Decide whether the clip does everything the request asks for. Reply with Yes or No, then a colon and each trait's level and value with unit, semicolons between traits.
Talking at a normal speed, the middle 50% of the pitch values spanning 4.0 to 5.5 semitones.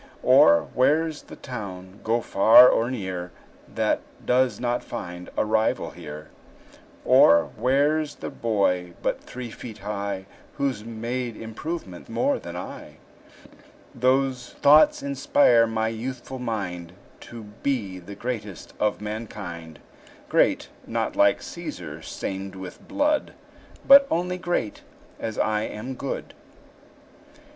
No: slow, 120 wpm; average, 4.8 semitones